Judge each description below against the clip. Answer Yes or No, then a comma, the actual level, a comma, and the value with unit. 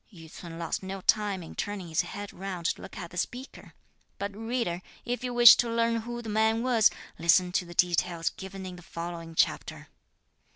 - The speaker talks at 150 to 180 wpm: No, average, 200 wpm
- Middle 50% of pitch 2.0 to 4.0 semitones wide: No, average, 4.6 semitones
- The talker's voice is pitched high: Yes, high, 195 Hz